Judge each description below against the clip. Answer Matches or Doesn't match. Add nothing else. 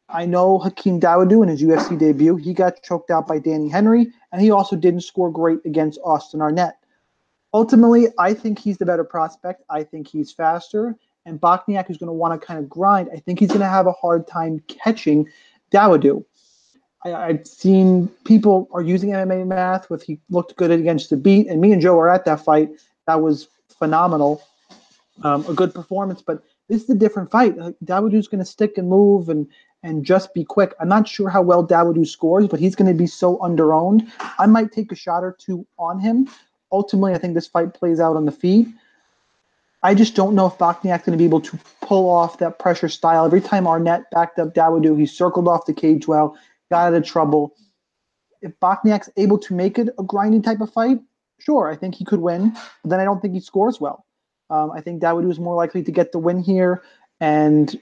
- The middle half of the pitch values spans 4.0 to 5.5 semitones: Doesn't match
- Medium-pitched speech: Matches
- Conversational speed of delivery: Doesn't match